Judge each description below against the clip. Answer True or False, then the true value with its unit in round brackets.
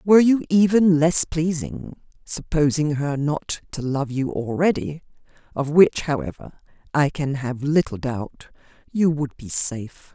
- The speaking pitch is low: False (150 Hz)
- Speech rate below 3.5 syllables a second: True (3.3 syllables/s)